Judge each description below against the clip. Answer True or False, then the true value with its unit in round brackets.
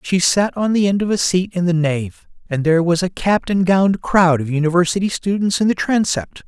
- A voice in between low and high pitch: True (180 Hz)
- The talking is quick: True (230 wpm)